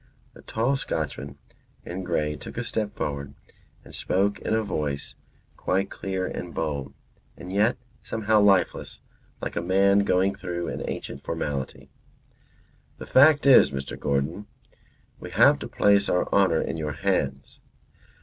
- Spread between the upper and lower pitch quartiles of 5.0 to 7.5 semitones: Yes, average, 5.3 semitones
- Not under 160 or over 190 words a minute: No, average, 145 wpm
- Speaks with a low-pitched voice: Yes, very low, 95 Hz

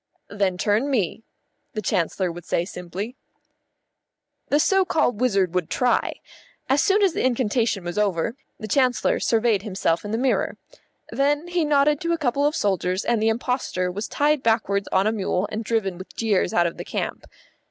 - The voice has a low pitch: No, high, 220 Hz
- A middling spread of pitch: No, wide, 5.9 semitones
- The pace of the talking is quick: No, average, 185 wpm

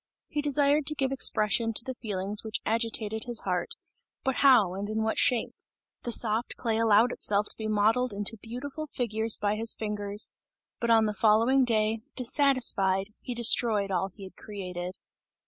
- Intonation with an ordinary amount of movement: Yes, average, 3.1 semitones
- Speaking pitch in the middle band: No, high, 220 Hz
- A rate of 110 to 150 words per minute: No, average, 170 wpm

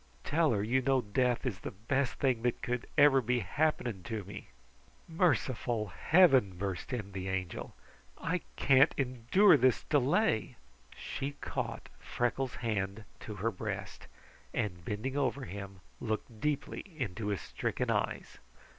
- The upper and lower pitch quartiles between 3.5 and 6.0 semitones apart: Yes, average, 4.8 semitones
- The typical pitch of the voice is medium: No, low, 120 Hz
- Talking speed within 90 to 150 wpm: Yes, average, 140 wpm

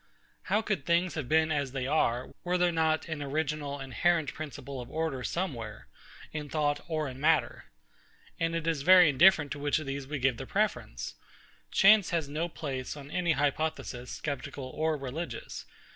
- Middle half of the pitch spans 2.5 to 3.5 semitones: Yes, average, 3.1 semitones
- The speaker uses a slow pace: No, average, 175 wpm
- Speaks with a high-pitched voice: No, medium, 150 Hz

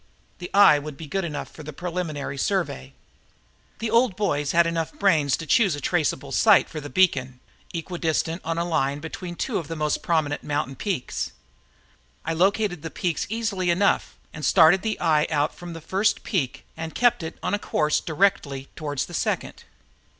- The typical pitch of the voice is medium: Yes, medium, 165 Hz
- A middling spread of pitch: Yes, average, 4.1 semitones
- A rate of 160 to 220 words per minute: Yes, average, 180 wpm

